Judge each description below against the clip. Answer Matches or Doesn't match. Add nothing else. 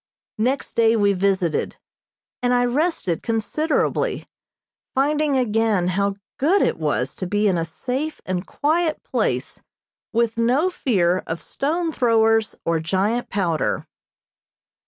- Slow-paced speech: Matches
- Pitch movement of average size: Doesn't match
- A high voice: Matches